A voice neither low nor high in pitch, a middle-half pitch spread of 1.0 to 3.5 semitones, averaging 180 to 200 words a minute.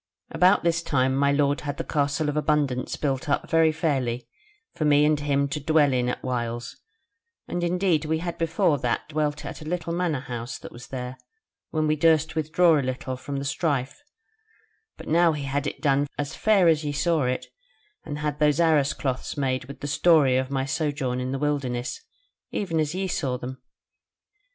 Yes: medium, 145 Hz; average, 3.1 semitones; average, 195 wpm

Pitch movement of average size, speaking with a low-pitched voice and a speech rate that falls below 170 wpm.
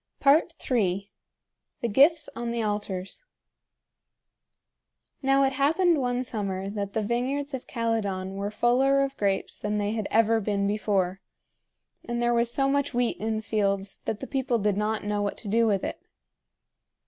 No: average, 4.2 semitones; high, 225 Hz; average, 160 wpm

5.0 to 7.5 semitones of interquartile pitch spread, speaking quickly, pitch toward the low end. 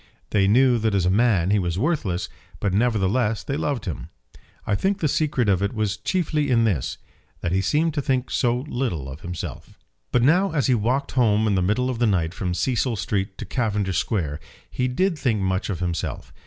Yes: average, 5.3 semitones; fast, 210 wpm; low, 110 Hz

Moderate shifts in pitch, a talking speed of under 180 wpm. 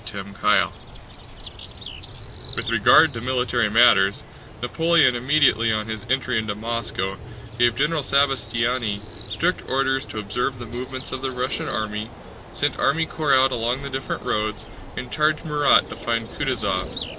Yes: average, 3.5 semitones; average, 145 wpm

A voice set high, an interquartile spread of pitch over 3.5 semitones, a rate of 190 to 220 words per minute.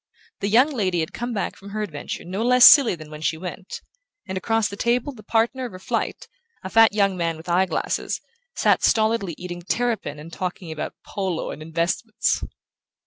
Yes: high, 195 Hz; average, 4.6 semitones; average, 195 wpm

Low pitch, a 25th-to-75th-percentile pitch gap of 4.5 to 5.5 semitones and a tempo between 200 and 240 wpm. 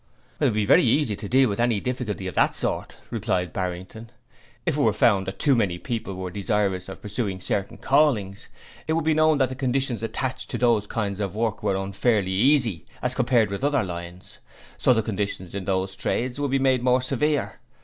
Yes: low, 110 Hz; average, 4.9 semitones; fast, 205 wpm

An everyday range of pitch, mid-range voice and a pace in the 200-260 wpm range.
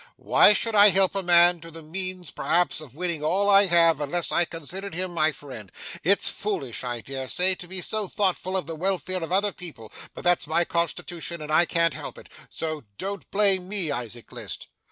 Yes: average, 3.3 semitones; medium, 175 Hz; fast, 205 wpm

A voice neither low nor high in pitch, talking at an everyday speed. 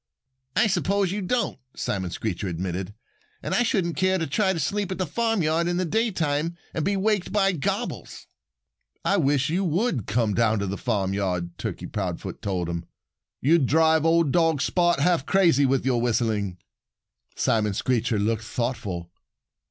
Yes: medium, 145 Hz; average, 160 wpm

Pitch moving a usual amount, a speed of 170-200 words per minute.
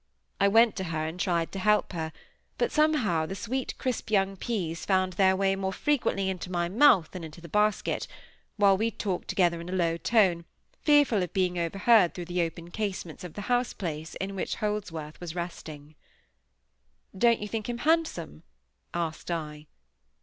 Yes: average, 3.9 semitones; average, 180 wpm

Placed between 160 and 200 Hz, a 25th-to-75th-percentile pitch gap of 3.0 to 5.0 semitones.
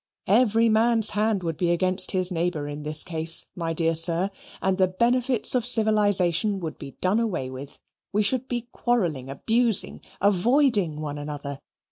No: medium, 185 Hz; wide, 5.5 semitones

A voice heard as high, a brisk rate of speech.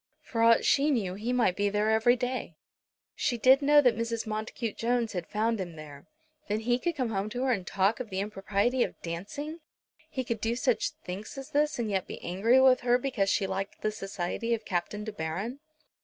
Yes: high, 225 Hz; fast, 215 wpm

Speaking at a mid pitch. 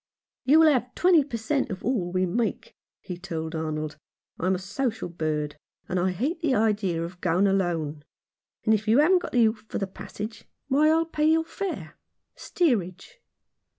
No: high, 215 Hz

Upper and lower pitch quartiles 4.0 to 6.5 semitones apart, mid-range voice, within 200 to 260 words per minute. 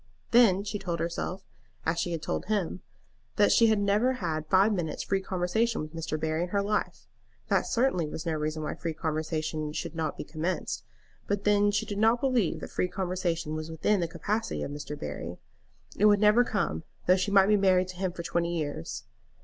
Yes: average, 4.4 semitones; medium, 180 Hz; fast, 205 wpm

